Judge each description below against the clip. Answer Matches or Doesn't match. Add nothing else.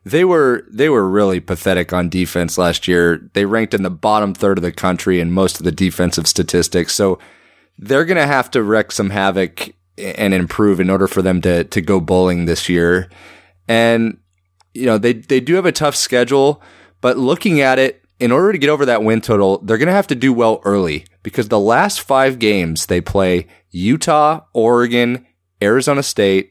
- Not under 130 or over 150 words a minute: Doesn't match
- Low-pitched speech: Matches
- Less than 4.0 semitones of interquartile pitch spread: Doesn't match